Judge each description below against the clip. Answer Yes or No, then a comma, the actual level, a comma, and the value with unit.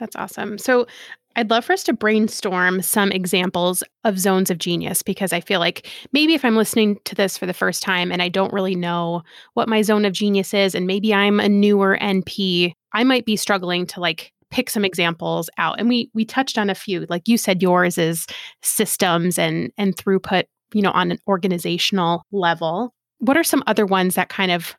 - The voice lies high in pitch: Yes, high, 195 Hz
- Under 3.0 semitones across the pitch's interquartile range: No, average, 3.3 semitones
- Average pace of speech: No, fast, 210 wpm